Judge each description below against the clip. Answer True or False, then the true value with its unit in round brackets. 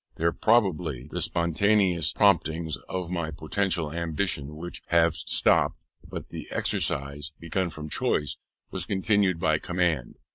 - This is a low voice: True (85 Hz)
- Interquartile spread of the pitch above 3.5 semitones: False (3.0 semitones)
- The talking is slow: True (130 wpm)